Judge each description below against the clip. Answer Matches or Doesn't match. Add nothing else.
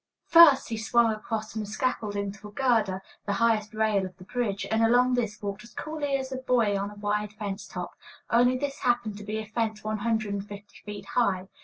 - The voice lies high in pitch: Matches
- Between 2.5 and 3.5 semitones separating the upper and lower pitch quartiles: Matches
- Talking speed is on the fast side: Matches